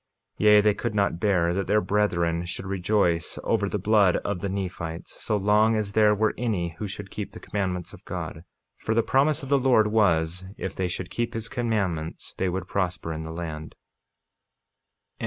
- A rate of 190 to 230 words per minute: Yes, average, 195 wpm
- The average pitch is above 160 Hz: No, low, 100 Hz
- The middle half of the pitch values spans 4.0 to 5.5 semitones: No, average, 3.4 semitones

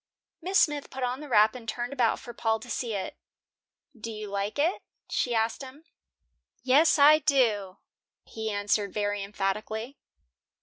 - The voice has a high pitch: Yes, high, 230 Hz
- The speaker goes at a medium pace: Yes, average, 160 wpm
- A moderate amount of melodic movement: Yes, average, 4.4 semitones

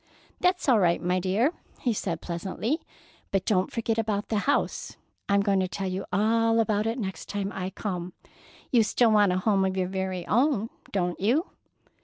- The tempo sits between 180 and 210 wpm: Yes, average, 185 wpm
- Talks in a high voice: Yes, high, 200 Hz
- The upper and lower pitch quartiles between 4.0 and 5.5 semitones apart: No, average, 3.4 semitones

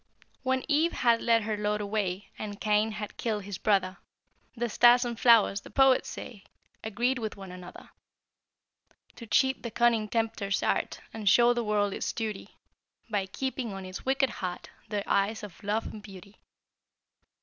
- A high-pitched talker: Yes, high, 215 Hz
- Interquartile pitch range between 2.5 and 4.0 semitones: Yes, average, 3.0 semitones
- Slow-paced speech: No, average, 165 wpm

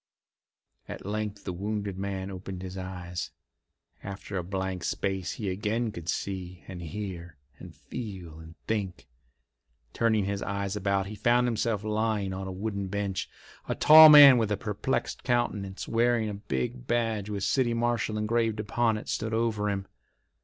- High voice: No, low, 105 Hz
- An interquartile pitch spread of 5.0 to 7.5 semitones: No, average, 2.9 semitones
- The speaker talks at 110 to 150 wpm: No, average, 160 wpm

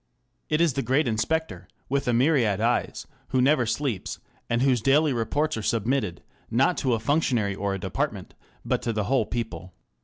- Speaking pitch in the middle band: No, low, 125 Hz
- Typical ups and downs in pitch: Yes, average, 4.0 semitones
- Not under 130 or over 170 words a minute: No, average, 180 wpm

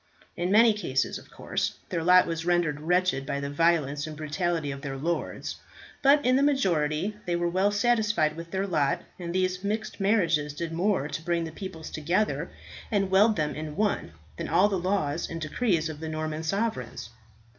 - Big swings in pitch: No, average, 4.3 semitones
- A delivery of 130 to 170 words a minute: No, average, 190 wpm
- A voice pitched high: No, medium, 170 Hz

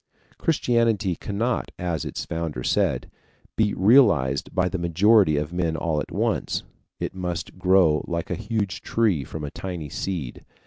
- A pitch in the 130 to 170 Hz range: No, very low, 90 Hz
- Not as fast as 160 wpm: Yes, average, 150 wpm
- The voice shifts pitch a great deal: No, average, 4.5 semitones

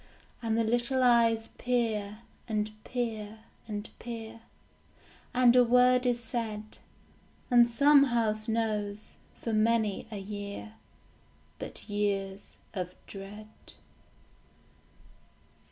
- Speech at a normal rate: No, slow, 100 wpm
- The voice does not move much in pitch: Yes, narrow, 2.3 semitones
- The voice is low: No, high, 225 Hz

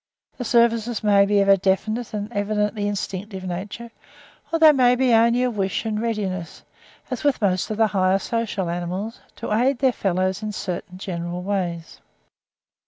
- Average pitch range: Yes, average, 3.6 semitones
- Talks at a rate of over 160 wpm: Yes, average, 170 wpm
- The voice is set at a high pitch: Yes, high, 205 Hz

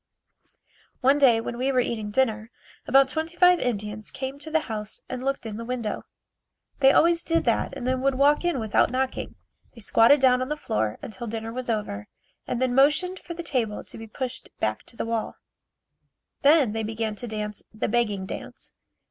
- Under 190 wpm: No, average, 195 wpm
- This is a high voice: Yes, high, 245 Hz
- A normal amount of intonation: Yes, average, 3.9 semitones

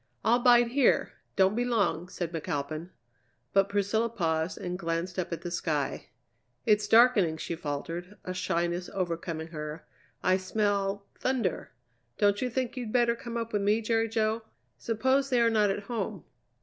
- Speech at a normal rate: Yes, average, 160 wpm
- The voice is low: No, high, 200 Hz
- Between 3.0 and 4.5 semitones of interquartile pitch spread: No, average, 5.0 semitones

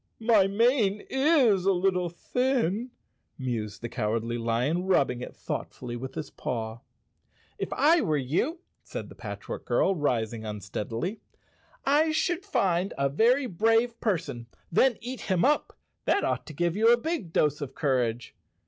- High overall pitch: No, medium, 180 Hz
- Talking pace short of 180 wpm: Yes, average, 160 wpm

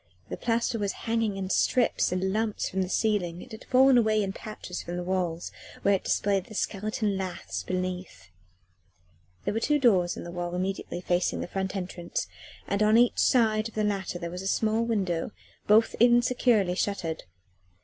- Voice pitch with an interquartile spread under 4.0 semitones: Yes, average, 3.4 semitones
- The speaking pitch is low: No, high, 195 Hz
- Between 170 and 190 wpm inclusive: Yes, average, 180 wpm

